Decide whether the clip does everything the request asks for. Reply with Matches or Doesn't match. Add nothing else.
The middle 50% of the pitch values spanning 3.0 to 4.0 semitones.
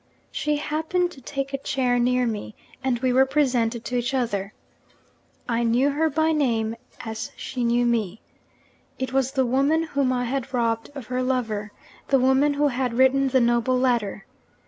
Doesn't match